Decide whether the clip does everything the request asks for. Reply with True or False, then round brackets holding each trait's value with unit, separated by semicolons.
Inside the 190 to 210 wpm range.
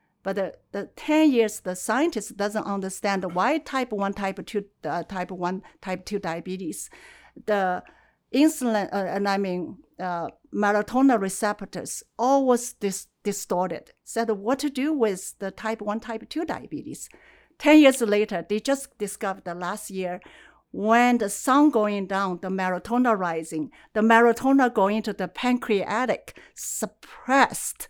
False (145 wpm)